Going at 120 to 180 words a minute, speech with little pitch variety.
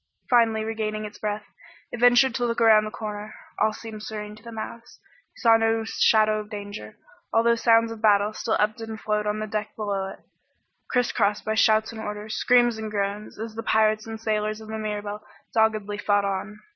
No: average, 200 wpm; narrow, 1.1 semitones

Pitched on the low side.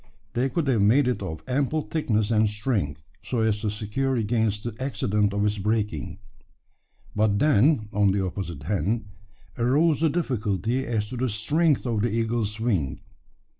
Yes: low, 110 Hz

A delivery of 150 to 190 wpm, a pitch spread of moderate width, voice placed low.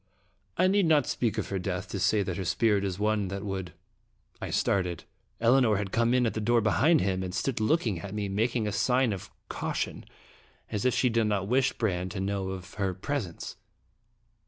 No: fast, 205 wpm; average, 3.8 semitones; low, 105 Hz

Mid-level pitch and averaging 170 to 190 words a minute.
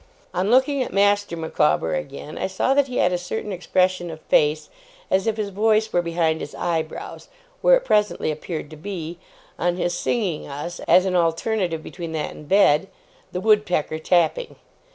Yes: medium, 180 Hz; average, 180 wpm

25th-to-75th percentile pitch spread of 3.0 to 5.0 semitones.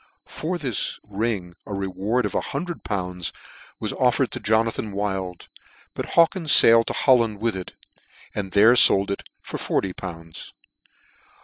Yes: average, 3.5 semitones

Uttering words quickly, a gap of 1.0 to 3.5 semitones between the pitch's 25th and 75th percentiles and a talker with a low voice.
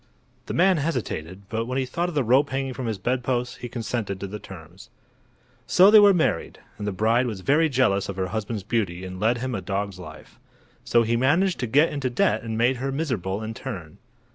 No: fast, 215 wpm; average, 5.1 semitones; low, 115 Hz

